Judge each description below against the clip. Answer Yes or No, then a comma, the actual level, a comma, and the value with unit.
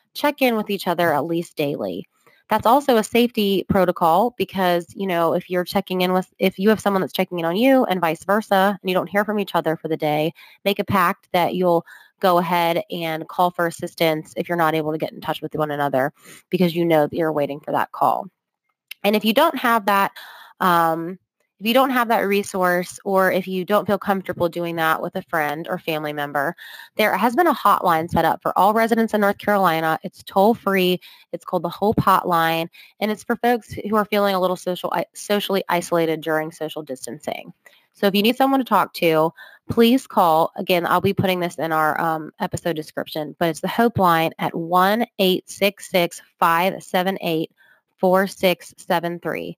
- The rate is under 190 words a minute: No, average, 200 wpm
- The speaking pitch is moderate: Yes, medium, 180 Hz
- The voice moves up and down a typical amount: Yes, average, 3.4 semitones